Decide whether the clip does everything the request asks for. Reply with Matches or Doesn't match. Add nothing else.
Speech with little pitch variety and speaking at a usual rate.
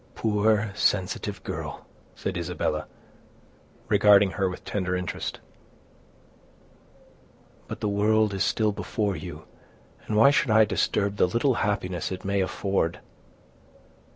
Doesn't match